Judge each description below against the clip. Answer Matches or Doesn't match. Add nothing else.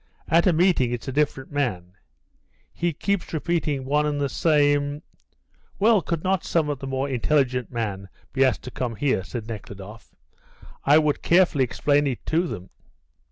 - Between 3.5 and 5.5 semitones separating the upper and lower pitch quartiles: Matches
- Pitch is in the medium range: Matches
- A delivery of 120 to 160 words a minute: Doesn't match